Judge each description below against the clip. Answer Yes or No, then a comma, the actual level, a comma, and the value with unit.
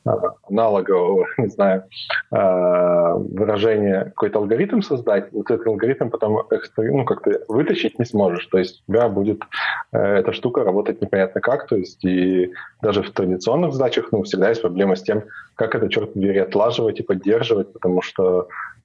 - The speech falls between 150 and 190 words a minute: Yes, average, 155 wpm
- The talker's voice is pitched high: No, very low, 95 Hz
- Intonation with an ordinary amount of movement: No, narrow, 2.2 semitones